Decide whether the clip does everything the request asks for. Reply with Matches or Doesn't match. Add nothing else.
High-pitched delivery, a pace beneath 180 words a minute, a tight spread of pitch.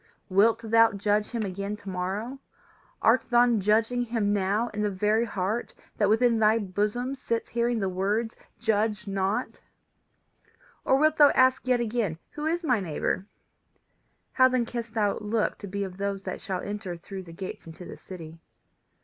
Doesn't match